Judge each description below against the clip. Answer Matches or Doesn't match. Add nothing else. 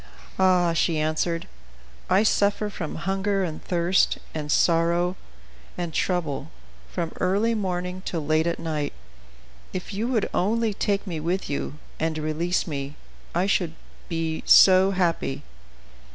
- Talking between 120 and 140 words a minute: Matches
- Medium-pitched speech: Matches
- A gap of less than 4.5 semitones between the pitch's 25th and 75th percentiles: Matches